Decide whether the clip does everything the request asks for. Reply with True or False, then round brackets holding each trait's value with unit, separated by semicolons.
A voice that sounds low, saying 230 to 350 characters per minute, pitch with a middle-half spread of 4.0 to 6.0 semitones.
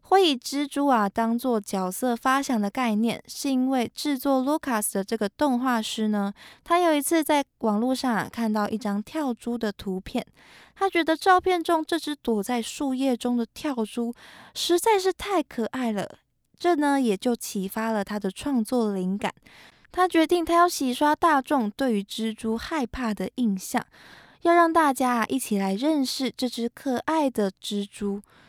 False (250 Hz; 255 characters per minute; 5.5 semitones)